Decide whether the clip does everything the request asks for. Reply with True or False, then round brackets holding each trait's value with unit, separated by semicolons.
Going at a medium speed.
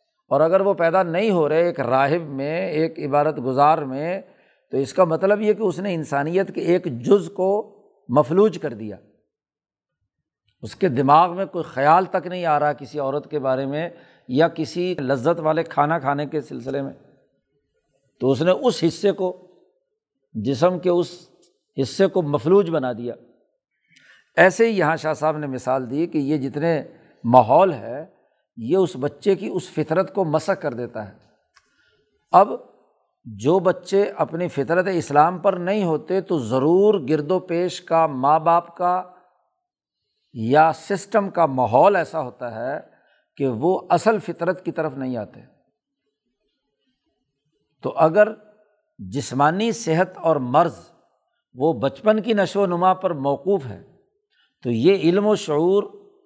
True (155 wpm)